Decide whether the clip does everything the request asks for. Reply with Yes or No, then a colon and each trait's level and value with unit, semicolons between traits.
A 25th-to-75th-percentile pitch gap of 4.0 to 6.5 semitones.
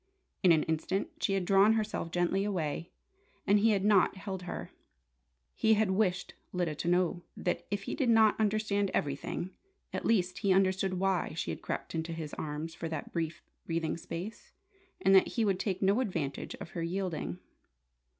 No: average, 3.3 semitones